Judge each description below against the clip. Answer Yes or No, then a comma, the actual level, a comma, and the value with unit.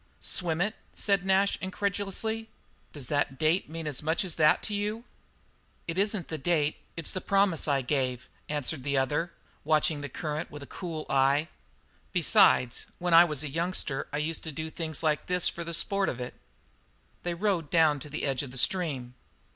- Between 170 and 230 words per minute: Yes, average, 185 wpm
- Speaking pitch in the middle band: Yes, medium, 160 Hz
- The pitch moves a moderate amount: Yes, average, 3.8 semitones